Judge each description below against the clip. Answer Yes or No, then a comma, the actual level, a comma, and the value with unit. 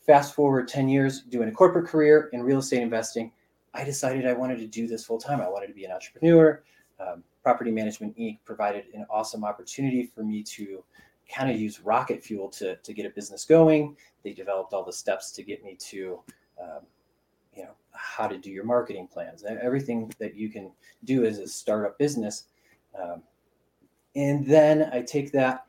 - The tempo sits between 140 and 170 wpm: No, average, 190 wpm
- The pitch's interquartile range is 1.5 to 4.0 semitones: No, average, 4.6 semitones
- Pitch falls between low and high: No, low, 125 Hz